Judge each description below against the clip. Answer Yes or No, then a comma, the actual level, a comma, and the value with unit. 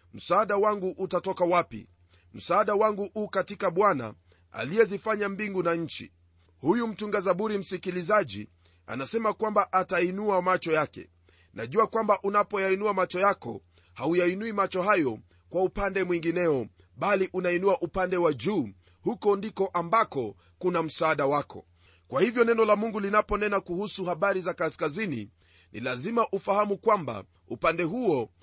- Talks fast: No, average, 130 wpm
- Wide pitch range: Yes, wide, 8.8 semitones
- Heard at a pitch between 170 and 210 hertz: Yes, medium, 185 Hz